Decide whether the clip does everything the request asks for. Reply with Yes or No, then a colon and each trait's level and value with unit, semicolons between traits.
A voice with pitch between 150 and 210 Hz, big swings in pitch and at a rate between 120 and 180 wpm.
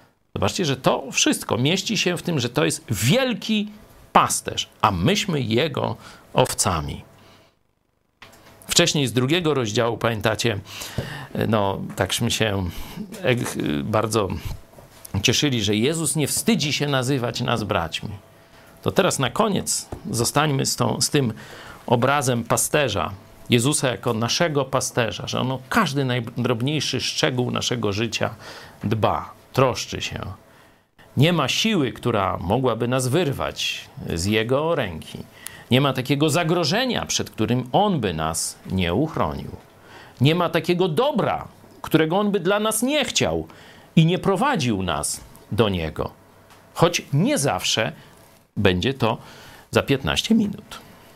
No: low, 130 Hz; wide, 6.3 semitones; average, 125 wpm